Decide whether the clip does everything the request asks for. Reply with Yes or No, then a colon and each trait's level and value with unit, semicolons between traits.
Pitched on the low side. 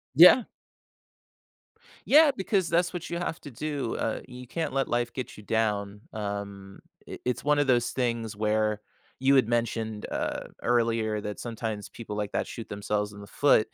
Yes: low, 115 Hz